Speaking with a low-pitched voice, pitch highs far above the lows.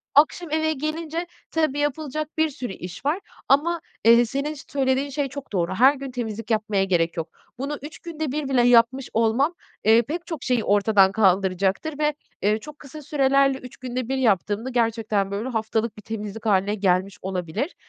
No: very high, 250 Hz; wide, 5.7 semitones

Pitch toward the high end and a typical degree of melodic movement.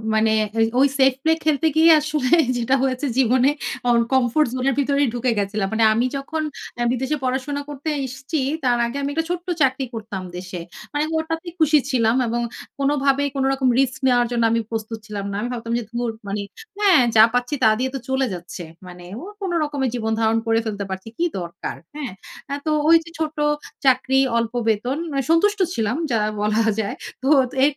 Yes: very high, 255 Hz; average, 4.1 semitones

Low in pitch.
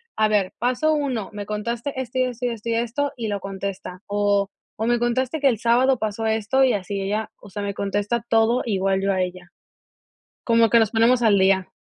No: high, 220 Hz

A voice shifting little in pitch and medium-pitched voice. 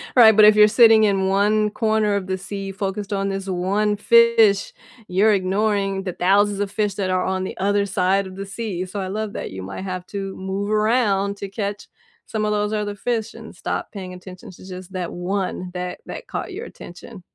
No: narrow, 2.0 semitones; high, 200 Hz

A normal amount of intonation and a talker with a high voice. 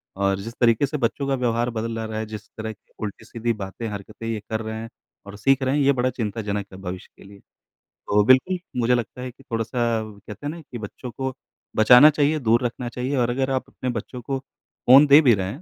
No: average, 3.3 semitones; low, 115 Hz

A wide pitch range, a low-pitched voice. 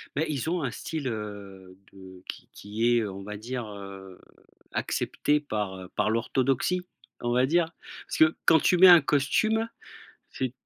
Yes: wide, 6.7 semitones; low, 120 Hz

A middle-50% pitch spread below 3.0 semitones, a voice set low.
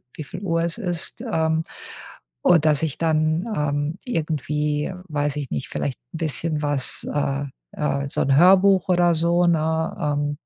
No: narrow, 2.5 semitones; medium, 155 Hz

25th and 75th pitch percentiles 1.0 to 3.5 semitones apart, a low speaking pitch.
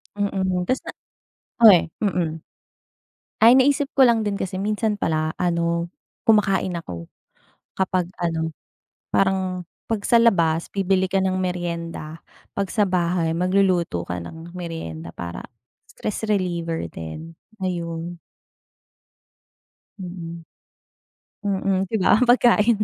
No: average, 3.1 semitones; medium, 180 Hz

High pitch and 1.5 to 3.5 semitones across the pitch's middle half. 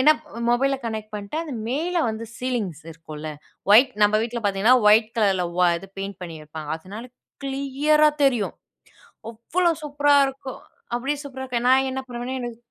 No: high, 240 Hz; average, 5.0 semitones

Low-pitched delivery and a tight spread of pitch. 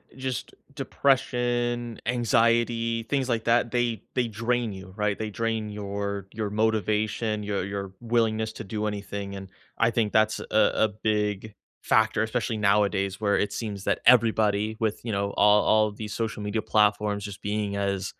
Yes: low, 110 Hz; narrow, 2.1 semitones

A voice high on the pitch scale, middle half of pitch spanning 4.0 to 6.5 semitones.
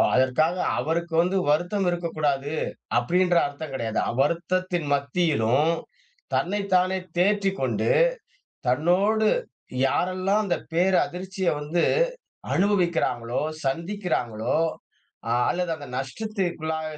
No: medium, 170 Hz; average, 4.3 semitones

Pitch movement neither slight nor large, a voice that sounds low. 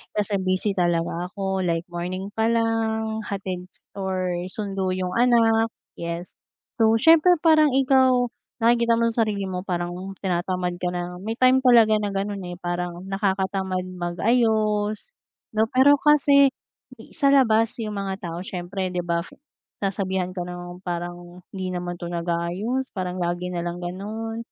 No: average, 4.0 semitones; high, 195 Hz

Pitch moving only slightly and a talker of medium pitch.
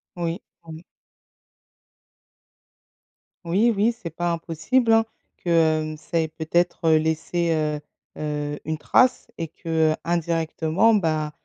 Yes: narrow, 1.7 semitones; medium, 165 Hz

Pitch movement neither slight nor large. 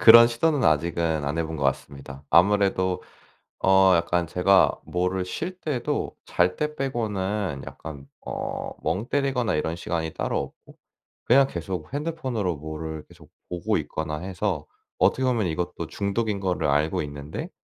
No: wide, 6.0 semitones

